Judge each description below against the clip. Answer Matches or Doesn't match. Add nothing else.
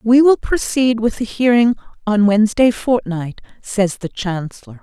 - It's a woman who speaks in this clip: Matches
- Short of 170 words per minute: Matches